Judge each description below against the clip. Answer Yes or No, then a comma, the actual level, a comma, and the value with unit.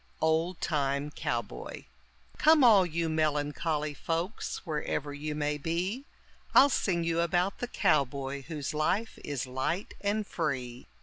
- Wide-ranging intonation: No, average, 3.5 semitones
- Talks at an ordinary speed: No, slow, 130 wpm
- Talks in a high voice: No, medium, 160 Hz